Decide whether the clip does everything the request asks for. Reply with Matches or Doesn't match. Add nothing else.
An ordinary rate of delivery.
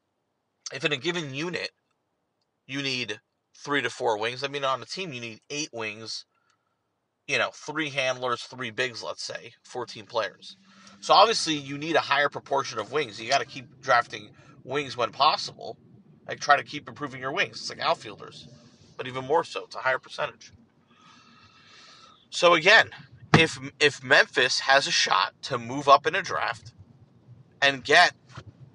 Matches